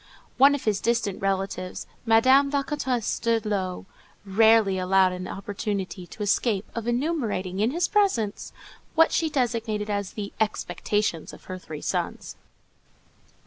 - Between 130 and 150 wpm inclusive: Yes, average, 140 wpm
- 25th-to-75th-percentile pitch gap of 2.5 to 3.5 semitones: No, average, 3.9 semitones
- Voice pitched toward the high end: Yes, high, 215 Hz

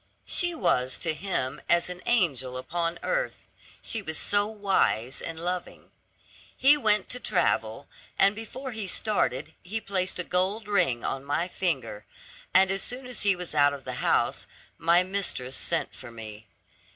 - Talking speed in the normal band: Yes, average, 165 wpm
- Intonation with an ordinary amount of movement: No, wide, 6.5 semitones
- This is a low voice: No, medium, 180 Hz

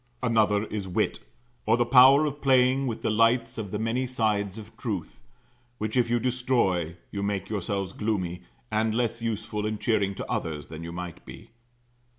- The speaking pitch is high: No, low, 110 Hz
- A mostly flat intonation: No, average, 3.3 semitones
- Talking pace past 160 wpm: Yes, average, 175 wpm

